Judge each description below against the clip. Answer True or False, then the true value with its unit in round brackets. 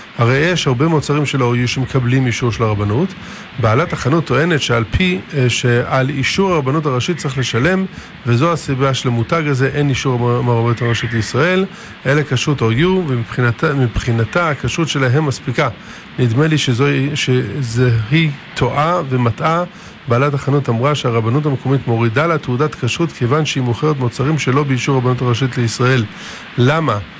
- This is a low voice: True (130 Hz)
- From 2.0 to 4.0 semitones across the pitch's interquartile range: True (3.7 semitones)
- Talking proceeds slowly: False (140 wpm)